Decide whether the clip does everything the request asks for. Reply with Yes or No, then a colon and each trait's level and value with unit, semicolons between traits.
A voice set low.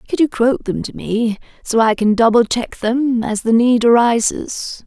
No: high, 230 Hz